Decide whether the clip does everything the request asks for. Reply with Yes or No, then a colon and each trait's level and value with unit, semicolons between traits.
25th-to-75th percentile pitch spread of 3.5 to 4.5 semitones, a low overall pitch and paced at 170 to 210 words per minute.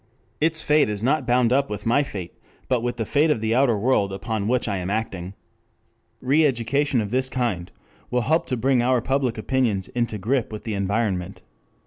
Yes: average, 4.0 semitones; low, 120 Hz; average, 200 wpm